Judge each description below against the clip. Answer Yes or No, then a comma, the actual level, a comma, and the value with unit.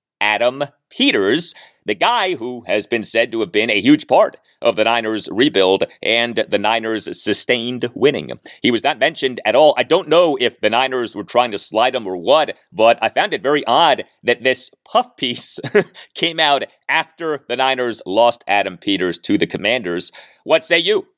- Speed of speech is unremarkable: Yes, average, 185 wpm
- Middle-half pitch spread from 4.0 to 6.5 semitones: Yes, average, 4.7 semitones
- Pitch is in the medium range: No, low, 120 Hz